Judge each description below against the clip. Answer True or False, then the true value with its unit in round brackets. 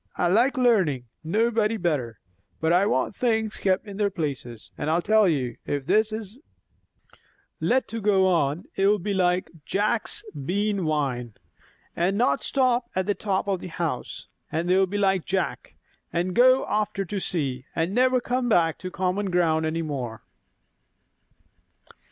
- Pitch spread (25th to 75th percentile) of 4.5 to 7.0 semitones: True (4.9 semitones)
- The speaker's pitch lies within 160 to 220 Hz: True (190 Hz)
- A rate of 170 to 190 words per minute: False (155 wpm)